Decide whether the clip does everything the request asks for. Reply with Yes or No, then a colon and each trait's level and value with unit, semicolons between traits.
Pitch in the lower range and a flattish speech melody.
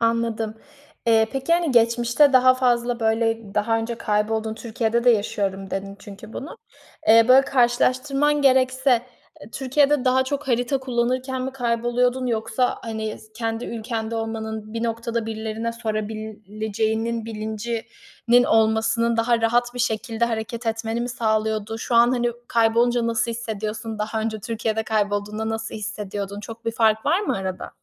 No: high, 230 Hz; narrow, 1.8 semitones